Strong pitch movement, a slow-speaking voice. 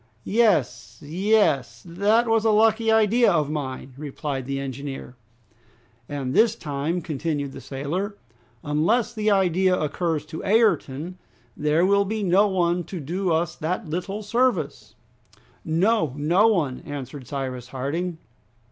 Yes: wide, 6.1 semitones; slow, 130 wpm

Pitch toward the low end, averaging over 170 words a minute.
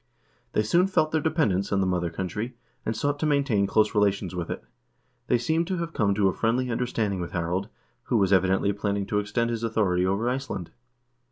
Yes: low, 105 Hz; average, 200 wpm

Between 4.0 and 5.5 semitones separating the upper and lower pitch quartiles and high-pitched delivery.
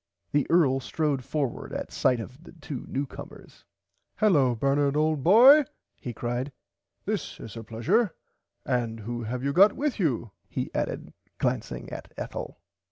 No: average, 4.7 semitones; low, 135 Hz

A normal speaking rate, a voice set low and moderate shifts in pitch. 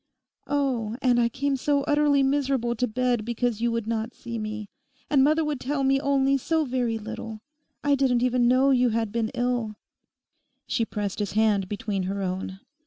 No: average, 180 wpm; high, 245 Hz; average, 3.6 semitones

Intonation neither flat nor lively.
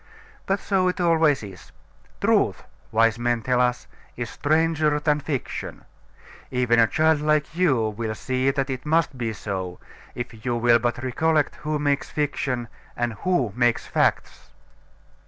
Yes: average, 4.4 semitones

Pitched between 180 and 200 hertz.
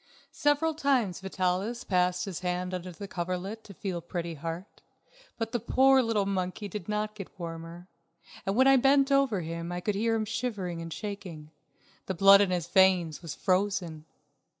Yes: high, 190 Hz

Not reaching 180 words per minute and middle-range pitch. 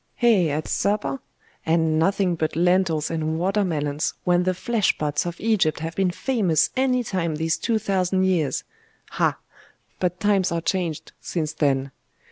Yes: average, 155 wpm; medium, 175 Hz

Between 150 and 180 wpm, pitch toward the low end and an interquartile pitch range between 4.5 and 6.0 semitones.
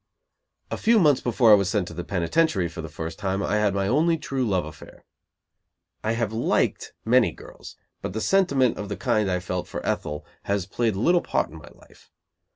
No: average, 200 wpm; low, 105 Hz; wide, 5.6 semitones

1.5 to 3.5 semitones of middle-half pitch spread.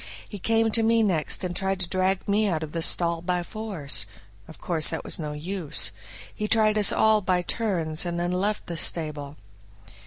No: average, 4.2 semitones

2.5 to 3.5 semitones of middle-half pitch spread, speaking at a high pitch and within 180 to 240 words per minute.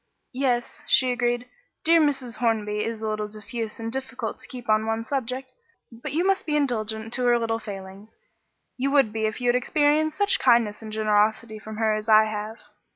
Yes: average, 2.9 semitones; high, 230 Hz; average, 195 wpm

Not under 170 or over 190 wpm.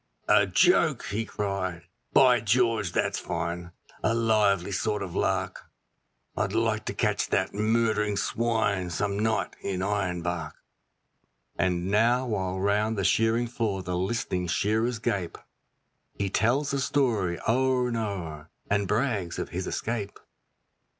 No: slow, 135 wpm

